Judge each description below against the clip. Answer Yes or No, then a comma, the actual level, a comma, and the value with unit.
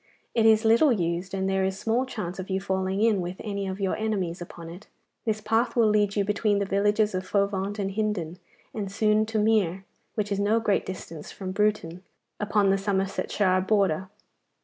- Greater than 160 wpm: Yes, average, 195 wpm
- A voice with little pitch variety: Yes, narrow, 2.0 semitones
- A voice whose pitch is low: No, high, 200 Hz